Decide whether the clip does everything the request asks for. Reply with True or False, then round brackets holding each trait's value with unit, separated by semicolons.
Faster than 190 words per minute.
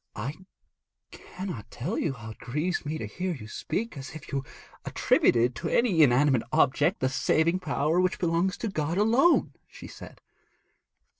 False (160 wpm)